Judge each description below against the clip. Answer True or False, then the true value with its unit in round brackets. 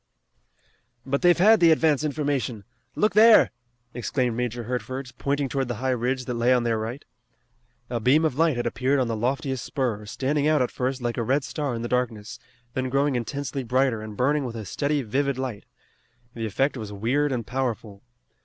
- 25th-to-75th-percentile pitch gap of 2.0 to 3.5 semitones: True (3.0 semitones)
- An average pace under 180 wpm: False (190 wpm)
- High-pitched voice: False (130 Hz)